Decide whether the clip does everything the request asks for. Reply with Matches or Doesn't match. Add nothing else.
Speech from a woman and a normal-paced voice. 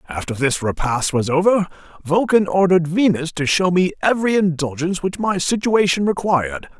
Doesn't match